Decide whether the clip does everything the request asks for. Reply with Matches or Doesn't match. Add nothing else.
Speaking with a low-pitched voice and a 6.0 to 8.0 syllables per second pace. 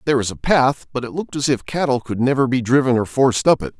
Matches